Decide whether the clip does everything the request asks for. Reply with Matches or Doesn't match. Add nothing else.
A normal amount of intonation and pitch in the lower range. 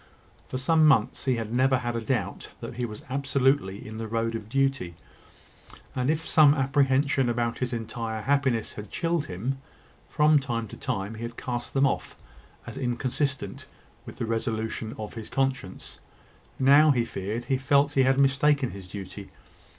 Matches